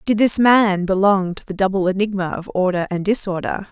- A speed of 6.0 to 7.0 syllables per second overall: No, 5.3 syllables/s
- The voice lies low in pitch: No, high, 195 Hz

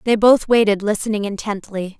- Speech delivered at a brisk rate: No, average, 150 wpm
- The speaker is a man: No, female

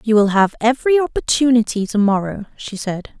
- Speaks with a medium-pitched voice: No, high, 225 Hz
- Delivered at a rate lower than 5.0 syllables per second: No, 5.5 syllables/s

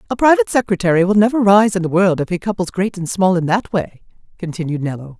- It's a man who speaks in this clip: No, female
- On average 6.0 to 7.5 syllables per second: Yes, 6.4 syllables/s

